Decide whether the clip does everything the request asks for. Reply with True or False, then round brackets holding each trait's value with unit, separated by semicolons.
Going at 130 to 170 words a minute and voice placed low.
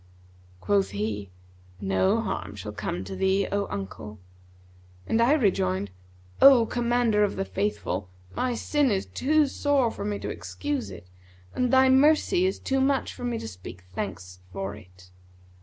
False (155 wpm; 195 Hz)